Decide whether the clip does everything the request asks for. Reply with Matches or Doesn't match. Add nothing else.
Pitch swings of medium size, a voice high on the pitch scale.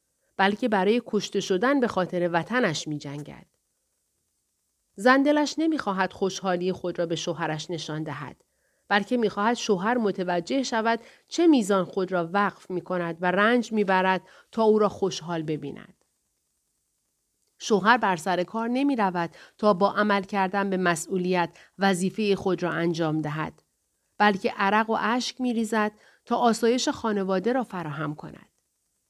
Matches